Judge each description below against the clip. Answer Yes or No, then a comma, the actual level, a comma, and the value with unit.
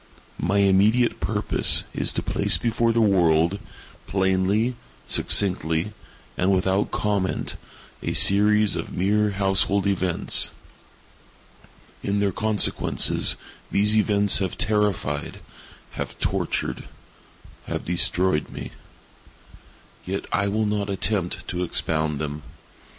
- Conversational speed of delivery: No, slow, 100 wpm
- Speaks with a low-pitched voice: Yes, low, 100 Hz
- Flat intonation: Yes, narrow, 2.3 semitones